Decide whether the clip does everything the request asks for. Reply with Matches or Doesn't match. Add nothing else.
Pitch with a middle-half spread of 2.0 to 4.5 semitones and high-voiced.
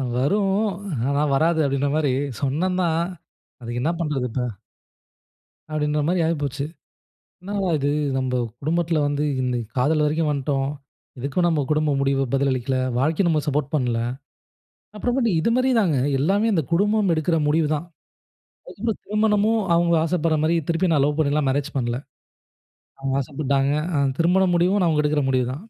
Doesn't match